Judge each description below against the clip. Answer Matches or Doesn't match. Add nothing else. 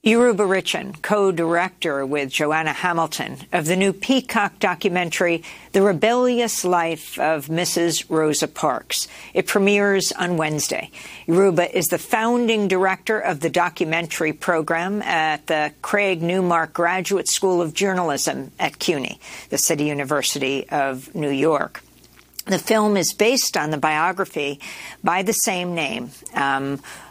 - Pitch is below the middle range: Doesn't match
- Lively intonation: Doesn't match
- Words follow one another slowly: Matches